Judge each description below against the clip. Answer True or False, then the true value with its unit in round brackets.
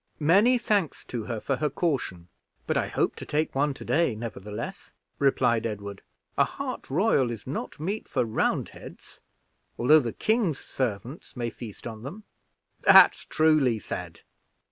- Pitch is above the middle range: False (130 Hz)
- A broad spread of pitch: True (5.7 semitones)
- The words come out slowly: False (150 wpm)